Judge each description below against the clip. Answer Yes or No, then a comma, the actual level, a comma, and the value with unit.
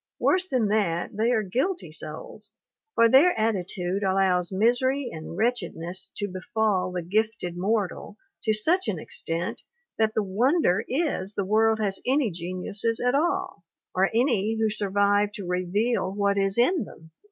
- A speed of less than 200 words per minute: Yes, average, 155 wpm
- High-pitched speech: Yes, high, 210 Hz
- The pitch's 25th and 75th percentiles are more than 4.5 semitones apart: No, average, 3.9 semitones